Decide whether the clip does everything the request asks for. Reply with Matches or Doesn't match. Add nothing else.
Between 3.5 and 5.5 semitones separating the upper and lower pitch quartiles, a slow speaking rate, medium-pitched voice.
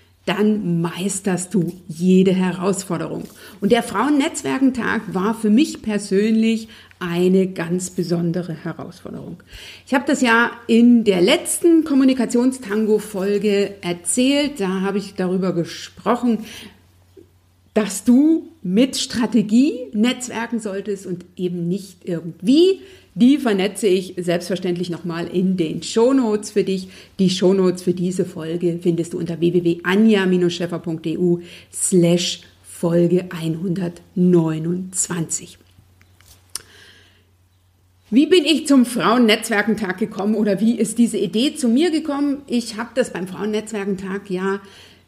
Doesn't match